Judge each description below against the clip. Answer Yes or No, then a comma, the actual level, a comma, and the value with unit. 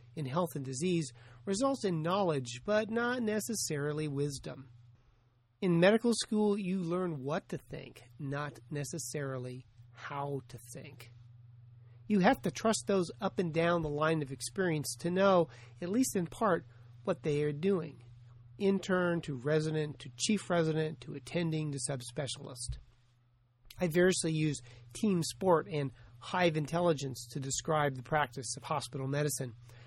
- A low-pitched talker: No, medium, 150 Hz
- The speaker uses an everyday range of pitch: No, wide, 6.3 semitones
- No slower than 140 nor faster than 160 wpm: Yes, average, 145 wpm